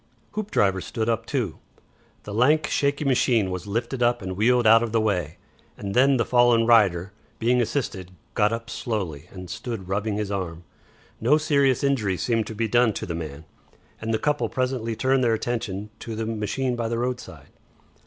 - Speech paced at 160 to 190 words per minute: Yes, average, 185 wpm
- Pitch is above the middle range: No, low, 115 Hz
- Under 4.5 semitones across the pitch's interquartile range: Yes, average, 3.6 semitones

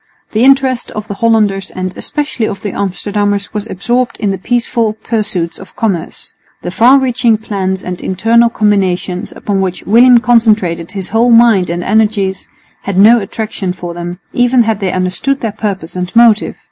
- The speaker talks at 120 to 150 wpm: No, average, 170 wpm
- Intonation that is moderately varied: Yes, average, 3.6 semitones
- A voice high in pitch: Yes, high, 210 Hz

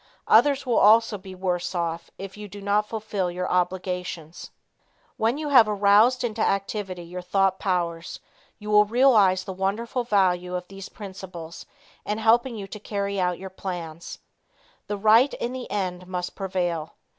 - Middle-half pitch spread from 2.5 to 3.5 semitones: Yes, average, 2.9 semitones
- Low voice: No, high, 195 Hz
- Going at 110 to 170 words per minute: Yes, average, 160 wpm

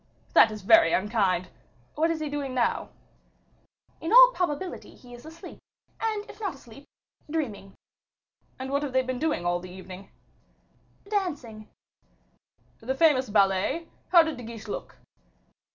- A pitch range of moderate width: No, wide, 7.1 semitones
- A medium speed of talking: Yes, average, 145 wpm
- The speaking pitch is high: Yes, very high, 260 Hz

